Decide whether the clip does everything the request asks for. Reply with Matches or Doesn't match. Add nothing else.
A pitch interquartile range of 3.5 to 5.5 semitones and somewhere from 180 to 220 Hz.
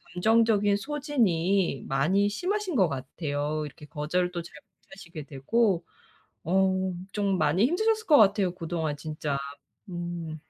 Matches